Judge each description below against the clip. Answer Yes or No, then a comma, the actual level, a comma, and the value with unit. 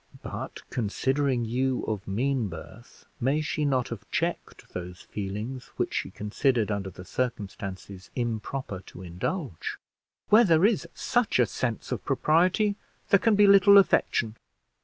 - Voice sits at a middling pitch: No, low, 125 Hz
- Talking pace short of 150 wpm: Yes, average, 140 wpm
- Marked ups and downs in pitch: Yes, wide, 7.4 semitones